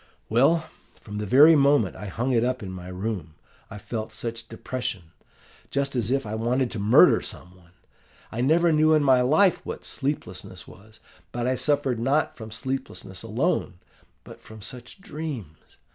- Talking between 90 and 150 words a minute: No, average, 170 wpm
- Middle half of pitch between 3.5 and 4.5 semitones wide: No, average, 4.9 semitones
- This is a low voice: Yes, low, 120 Hz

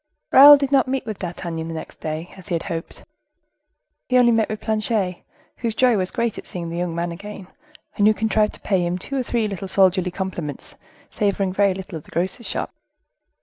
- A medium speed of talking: No, fast, 210 wpm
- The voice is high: Yes, high, 195 Hz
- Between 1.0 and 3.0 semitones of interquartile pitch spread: No, average, 4.1 semitones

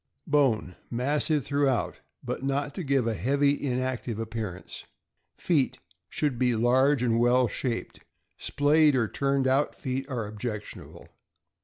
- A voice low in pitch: Yes, low, 130 Hz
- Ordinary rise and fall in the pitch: Yes, average, 3.3 semitones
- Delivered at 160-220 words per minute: No, average, 140 wpm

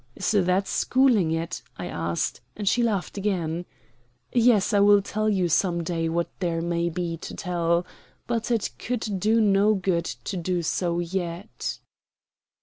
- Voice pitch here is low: No, medium, 180 Hz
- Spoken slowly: No, average, 155 wpm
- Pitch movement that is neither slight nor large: Yes, average, 3.5 semitones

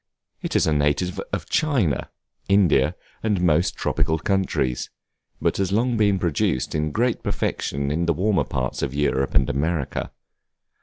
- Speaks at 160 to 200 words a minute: No, average, 150 wpm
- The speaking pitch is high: No, very low, 85 Hz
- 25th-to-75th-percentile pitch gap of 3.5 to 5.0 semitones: No, wide, 5.6 semitones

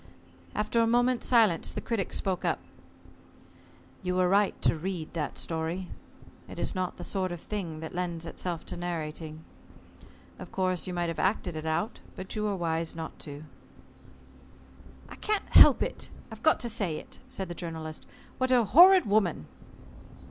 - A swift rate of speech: No, average, 165 wpm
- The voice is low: No, medium, 180 Hz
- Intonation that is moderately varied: Yes, average, 4.3 semitones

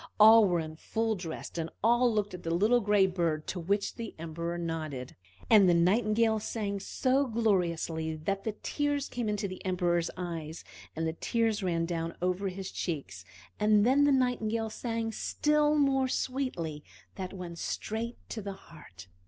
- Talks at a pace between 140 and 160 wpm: No, average, 170 wpm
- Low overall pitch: No, high, 195 Hz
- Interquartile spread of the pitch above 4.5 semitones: Yes, average, 5.2 semitones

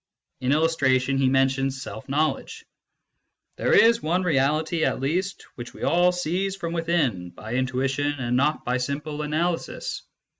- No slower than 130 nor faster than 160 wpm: Yes, average, 150 wpm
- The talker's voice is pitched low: No, medium, 145 Hz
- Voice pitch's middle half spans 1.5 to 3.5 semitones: No, average, 4.1 semitones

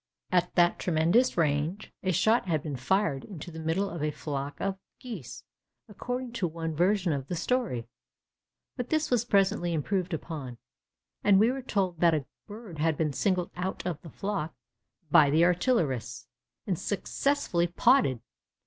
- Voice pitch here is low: No, medium, 175 Hz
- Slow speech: No, average, 160 wpm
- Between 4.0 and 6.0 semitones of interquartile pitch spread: Yes, average, 4.7 semitones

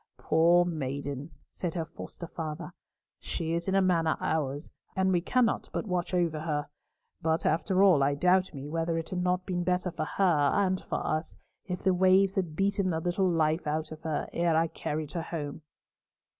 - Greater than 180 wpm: Yes, average, 190 wpm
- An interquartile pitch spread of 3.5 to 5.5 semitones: No, average, 2.7 semitones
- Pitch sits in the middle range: Yes, medium, 170 Hz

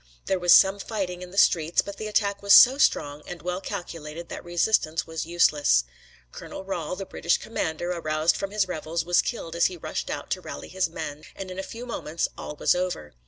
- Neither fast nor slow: No, fast, 210 wpm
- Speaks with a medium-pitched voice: Yes, medium, 175 Hz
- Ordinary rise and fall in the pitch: Yes, average, 3.3 semitones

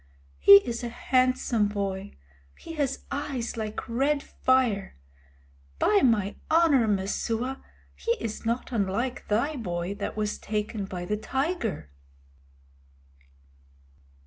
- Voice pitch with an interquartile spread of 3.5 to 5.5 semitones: Yes, average, 4.2 semitones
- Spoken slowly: Yes, slow, 115 wpm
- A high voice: Yes, high, 230 Hz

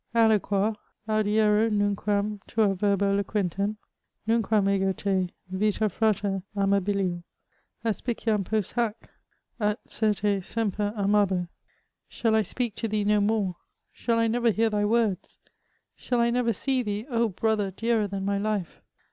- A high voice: Yes, high, 210 Hz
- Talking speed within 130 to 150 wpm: Yes, average, 140 wpm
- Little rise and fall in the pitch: Yes, narrow, 2.0 semitones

